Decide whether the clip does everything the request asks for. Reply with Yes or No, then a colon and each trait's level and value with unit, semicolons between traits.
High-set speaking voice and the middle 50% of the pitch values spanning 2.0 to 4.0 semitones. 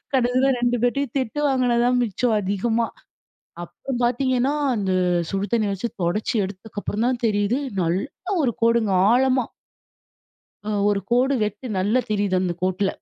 Yes: high, 230 Hz; average, 3.7 semitones